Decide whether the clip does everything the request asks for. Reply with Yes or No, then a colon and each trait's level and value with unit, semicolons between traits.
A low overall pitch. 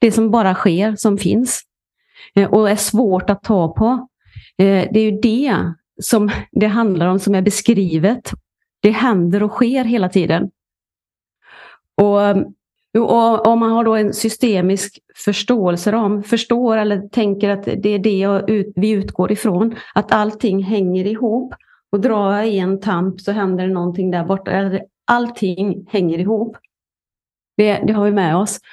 No: high, 205 Hz